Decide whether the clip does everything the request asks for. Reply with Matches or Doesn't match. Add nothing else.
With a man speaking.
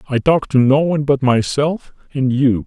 Matches